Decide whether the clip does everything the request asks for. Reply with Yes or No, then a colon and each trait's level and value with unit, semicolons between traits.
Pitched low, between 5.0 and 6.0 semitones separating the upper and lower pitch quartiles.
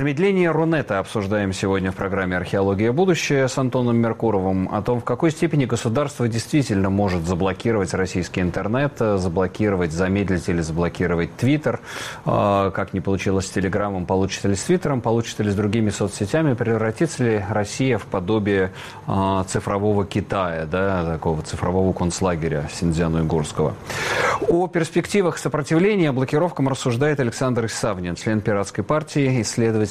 Yes: low, 105 Hz; average, 5.3 semitones